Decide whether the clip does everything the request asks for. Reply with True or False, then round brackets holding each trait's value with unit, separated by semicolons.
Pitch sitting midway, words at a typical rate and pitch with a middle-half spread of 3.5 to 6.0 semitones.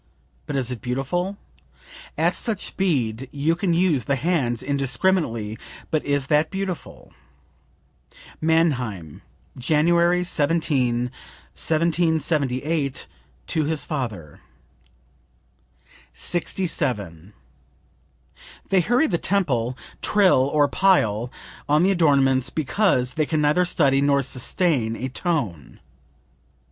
False (145 Hz; 100 wpm; 5.2 semitones)